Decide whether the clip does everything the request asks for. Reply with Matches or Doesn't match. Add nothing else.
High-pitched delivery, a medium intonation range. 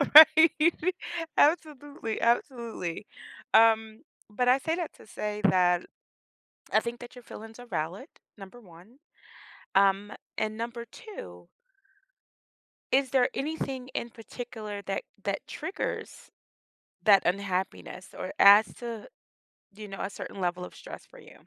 Matches